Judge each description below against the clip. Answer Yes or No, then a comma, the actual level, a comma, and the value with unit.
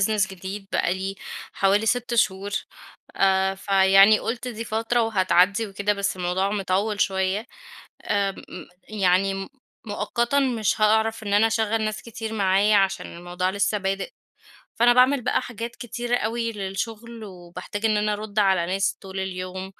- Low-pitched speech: No, high, 205 Hz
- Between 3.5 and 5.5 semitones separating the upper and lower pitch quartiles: No, narrow, 2.6 semitones